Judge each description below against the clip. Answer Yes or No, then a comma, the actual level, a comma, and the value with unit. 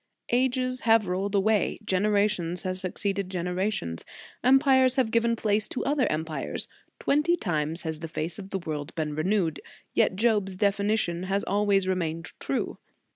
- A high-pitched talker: Yes, high, 195 Hz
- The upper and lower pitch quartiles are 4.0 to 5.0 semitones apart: Yes, average, 4.3 semitones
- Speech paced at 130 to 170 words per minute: Yes, average, 155 wpm